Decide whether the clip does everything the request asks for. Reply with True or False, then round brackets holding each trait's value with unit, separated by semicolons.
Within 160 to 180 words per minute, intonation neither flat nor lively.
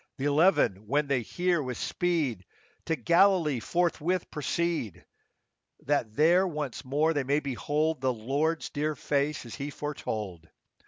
False (140 wpm; 4.1 semitones)